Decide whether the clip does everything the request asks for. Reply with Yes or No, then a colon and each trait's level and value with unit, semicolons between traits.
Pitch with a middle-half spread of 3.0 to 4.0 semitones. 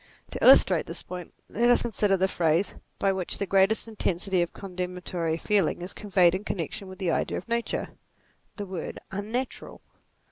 No: narrow, 2.5 semitones